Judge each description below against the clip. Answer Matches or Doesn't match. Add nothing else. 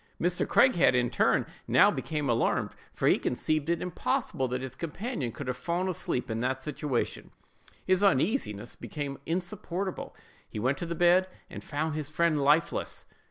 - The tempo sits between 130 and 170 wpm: Matches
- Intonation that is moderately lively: Matches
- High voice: Doesn't match